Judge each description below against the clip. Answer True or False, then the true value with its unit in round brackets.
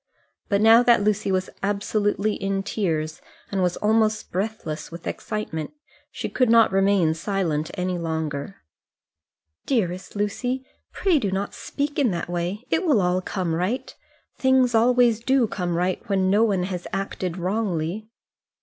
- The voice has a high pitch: True (195 Hz)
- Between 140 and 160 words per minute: True (150 wpm)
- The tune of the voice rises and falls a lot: False (3.8 semitones)